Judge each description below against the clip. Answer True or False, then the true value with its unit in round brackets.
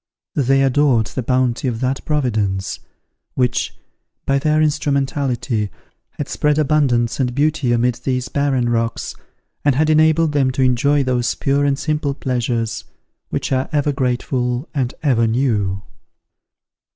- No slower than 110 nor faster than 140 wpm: True (135 wpm)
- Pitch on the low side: True (130 Hz)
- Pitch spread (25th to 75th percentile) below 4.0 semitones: True (2.9 semitones)